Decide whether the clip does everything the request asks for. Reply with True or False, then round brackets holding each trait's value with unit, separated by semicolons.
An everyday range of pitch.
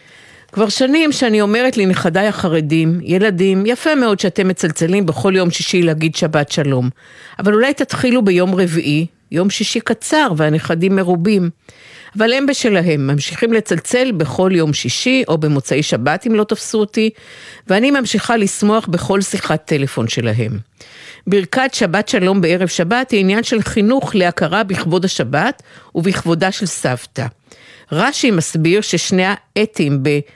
True (5.0 semitones)